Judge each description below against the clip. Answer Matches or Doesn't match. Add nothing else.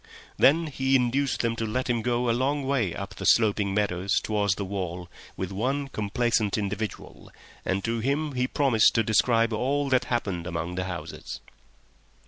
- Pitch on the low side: Matches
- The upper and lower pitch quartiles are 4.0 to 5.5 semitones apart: Matches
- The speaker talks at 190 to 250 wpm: Doesn't match